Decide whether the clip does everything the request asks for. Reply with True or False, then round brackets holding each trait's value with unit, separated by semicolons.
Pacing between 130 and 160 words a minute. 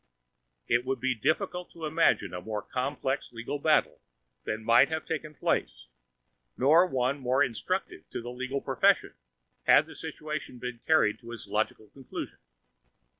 True (150 wpm)